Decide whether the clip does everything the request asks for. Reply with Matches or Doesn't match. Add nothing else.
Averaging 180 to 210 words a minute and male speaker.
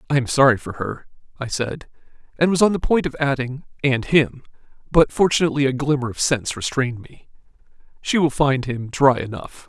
Matches